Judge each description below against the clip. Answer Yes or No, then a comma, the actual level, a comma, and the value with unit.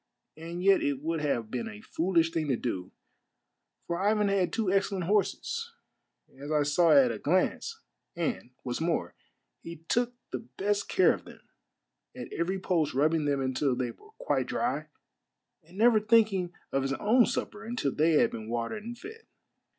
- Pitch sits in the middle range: Yes, medium, 170 Hz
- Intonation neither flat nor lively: No, wide, 6.6 semitones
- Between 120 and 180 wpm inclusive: Yes, average, 175 wpm